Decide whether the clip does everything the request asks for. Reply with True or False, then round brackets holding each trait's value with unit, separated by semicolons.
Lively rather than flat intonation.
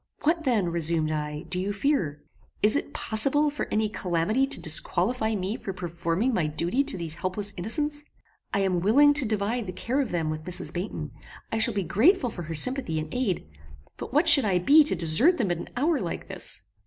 True (7.5 semitones)